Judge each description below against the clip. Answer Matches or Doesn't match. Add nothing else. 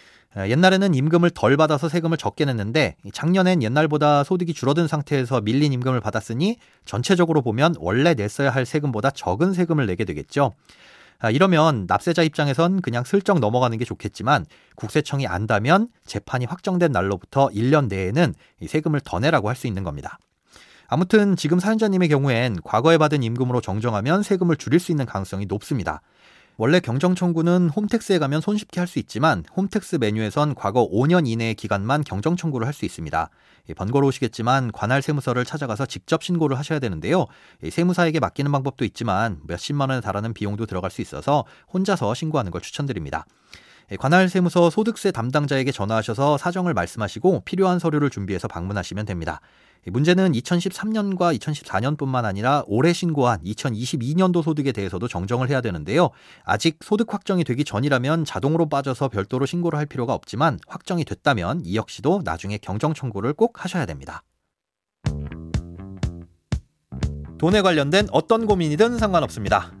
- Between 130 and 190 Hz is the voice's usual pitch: Matches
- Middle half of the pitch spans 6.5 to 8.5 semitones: Matches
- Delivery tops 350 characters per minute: Matches